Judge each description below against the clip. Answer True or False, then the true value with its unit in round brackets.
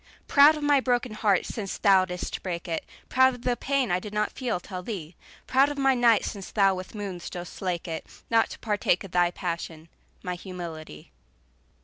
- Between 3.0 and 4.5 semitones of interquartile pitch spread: False (5.4 semitones)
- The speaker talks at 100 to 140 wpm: False (195 wpm)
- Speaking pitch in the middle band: False (195 Hz)